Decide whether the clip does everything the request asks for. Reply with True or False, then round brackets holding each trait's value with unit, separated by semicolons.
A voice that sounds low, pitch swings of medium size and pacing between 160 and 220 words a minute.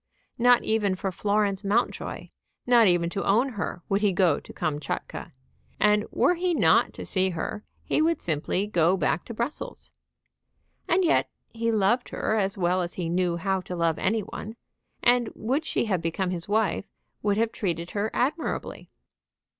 False (200 Hz; 4.2 semitones; 170 wpm)